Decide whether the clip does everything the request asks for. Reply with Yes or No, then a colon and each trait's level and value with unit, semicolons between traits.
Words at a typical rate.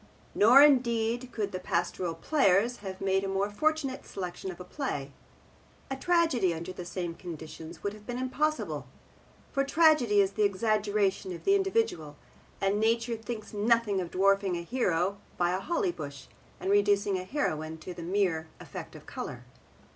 Yes: average, 165 wpm